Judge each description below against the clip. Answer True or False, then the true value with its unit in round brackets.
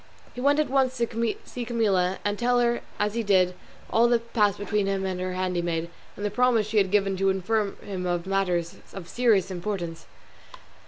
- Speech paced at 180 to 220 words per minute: True (200 wpm)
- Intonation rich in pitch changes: False (4.0 semitones)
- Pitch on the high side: True (200 Hz)